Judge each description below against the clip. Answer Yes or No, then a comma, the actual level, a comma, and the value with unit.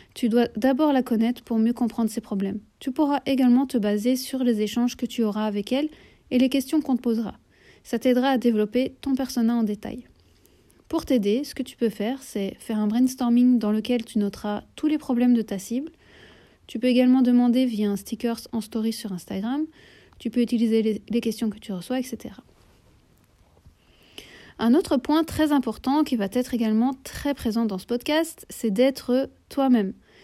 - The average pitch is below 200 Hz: No, high, 240 Hz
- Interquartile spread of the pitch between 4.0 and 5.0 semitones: No, average, 2.7 semitones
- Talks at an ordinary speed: Yes, average, 190 wpm